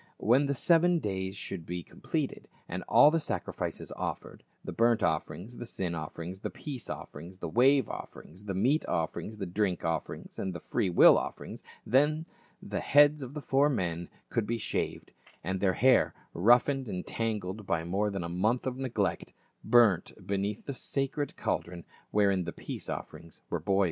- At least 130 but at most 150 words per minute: No, average, 175 wpm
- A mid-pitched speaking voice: No, low, 105 Hz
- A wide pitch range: Yes, wide, 6.4 semitones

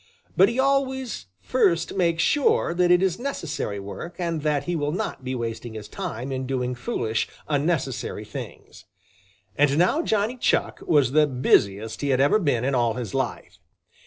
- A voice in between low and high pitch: Yes, medium, 145 Hz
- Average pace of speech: Yes, average, 170 wpm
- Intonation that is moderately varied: No, wide, 6.4 semitones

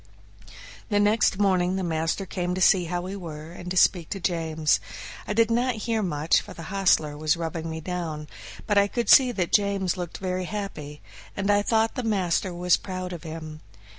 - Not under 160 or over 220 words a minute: Yes, average, 195 wpm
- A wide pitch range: No, average, 3.5 semitones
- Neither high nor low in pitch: Yes, medium, 180 Hz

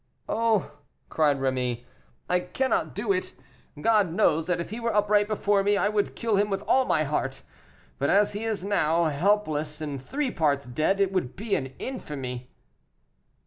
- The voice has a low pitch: No, high, 190 Hz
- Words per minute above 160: Yes, average, 175 wpm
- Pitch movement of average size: No, wide, 6.1 semitones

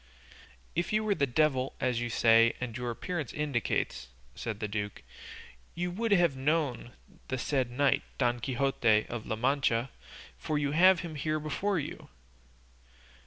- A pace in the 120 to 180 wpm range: Yes, average, 160 wpm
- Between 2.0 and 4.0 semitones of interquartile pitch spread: No, average, 4.6 semitones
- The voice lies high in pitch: No, low, 135 Hz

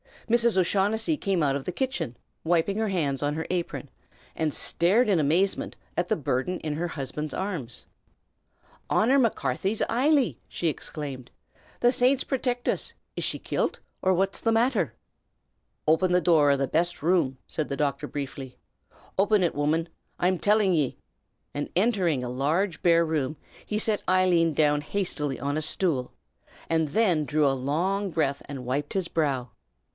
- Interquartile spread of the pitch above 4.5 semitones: Yes, average, 5.3 semitones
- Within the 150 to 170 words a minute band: Yes, average, 160 wpm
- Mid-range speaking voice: Yes, medium, 170 Hz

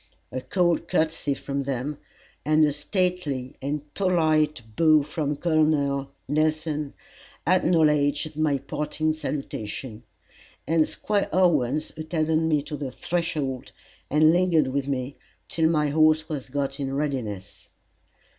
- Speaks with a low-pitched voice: No, medium, 150 Hz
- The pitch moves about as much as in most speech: No, narrow, 2.2 semitones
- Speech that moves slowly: Yes, slow, 120 wpm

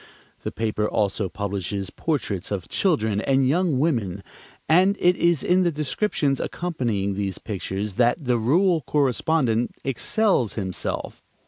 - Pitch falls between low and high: No, low, 125 Hz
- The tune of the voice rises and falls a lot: Yes, wide, 8.0 semitones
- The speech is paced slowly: Yes, slow, 130 wpm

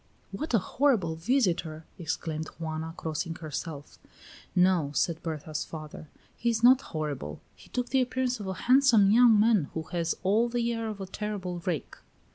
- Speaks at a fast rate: No, average, 165 wpm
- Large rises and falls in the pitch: Yes, wide, 6.6 semitones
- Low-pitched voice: No, medium, 185 Hz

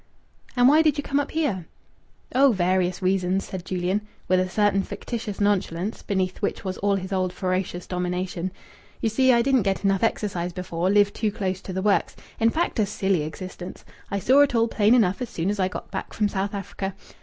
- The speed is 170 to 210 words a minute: Yes, fast, 205 wpm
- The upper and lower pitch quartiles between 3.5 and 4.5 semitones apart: No, average, 3.1 semitones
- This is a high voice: Yes, high, 195 Hz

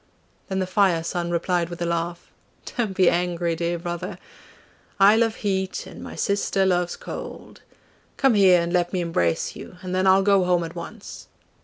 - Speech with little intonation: Yes, narrow, 2.0 semitones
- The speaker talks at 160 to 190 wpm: Yes, average, 180 wpm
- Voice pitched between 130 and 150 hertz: No, medium, 180 Hz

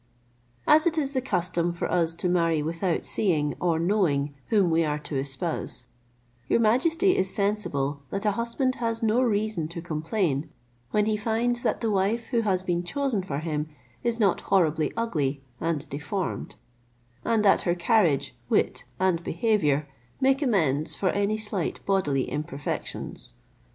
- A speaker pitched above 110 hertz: Yes, medium, 185 Hz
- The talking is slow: No, average, 155 wpm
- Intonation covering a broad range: Yes, wide, 5.9 semitones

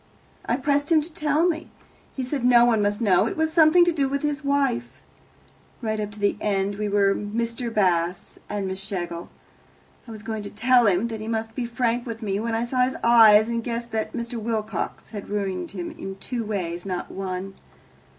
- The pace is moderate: No, fast, 210 wpm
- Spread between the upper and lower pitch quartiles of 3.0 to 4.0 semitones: Yes, average, 3.7 semitones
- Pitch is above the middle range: Yes, high, 225 Hz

